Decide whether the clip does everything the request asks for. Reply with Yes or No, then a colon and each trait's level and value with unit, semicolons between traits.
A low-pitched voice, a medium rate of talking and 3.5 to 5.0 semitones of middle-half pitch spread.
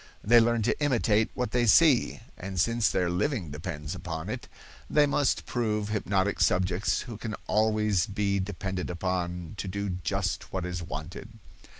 Yes: low, 100 Hz; average, 160 wpm; average, 3.8 semitones